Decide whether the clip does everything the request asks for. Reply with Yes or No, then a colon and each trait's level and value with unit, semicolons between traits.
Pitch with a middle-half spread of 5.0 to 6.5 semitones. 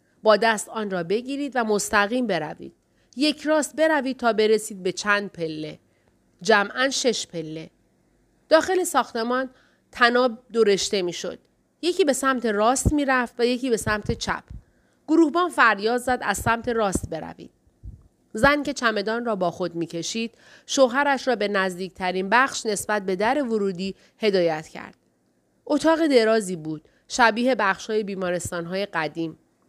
Yes: average, 5.3 semitones